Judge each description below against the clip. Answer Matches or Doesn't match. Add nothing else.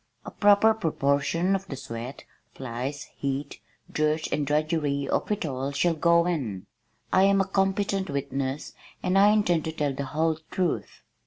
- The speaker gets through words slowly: Doesn't match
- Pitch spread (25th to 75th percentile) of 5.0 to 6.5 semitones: Matches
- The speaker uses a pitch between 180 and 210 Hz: Doesn't match